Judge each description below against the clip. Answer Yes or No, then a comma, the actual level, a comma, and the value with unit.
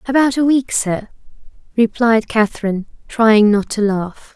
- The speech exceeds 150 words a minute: No, average, 140 wpm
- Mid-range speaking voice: No, high, 225 Hz